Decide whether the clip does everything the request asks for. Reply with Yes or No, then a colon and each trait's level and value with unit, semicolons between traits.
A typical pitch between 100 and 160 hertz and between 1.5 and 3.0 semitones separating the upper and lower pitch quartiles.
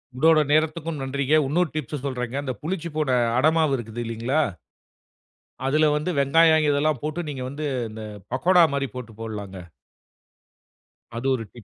No: medium, 140 Hz; average, 3.7 semitones